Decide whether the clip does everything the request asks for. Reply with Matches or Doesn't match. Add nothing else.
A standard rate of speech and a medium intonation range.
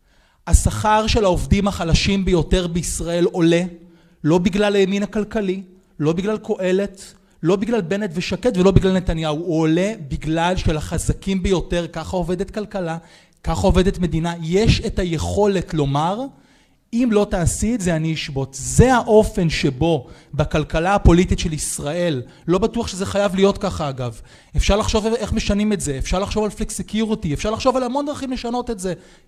Doesn't match